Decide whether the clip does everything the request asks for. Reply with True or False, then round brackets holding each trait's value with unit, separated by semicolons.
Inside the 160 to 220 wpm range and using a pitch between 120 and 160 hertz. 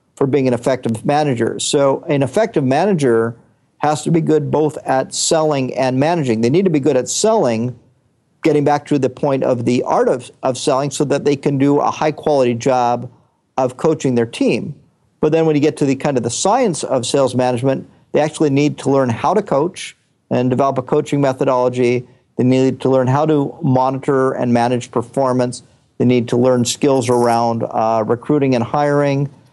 True (195 wpm; 135 Hz)